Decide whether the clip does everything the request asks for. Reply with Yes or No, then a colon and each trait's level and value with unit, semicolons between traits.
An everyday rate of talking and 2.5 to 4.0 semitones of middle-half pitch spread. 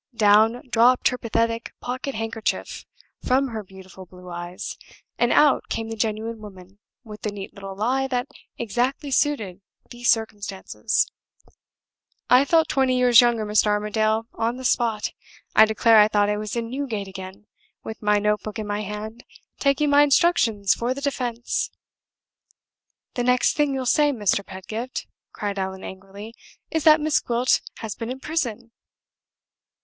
Yes: average, 155 wpm; average, 3.3 semitones